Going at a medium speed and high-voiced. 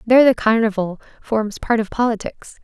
Yes: average, 160 wpm; high, 220 Hz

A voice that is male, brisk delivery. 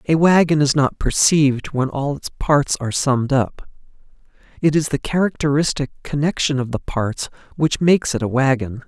No: male; average, 170 wpm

